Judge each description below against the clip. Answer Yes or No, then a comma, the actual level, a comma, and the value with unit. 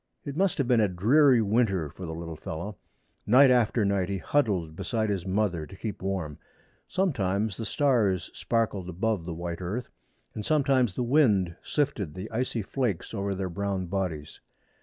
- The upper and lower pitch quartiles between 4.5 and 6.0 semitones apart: Yes, average, 4.9 semitones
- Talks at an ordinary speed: Yes, average, 170 wpm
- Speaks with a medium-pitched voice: No, low, 100 Hz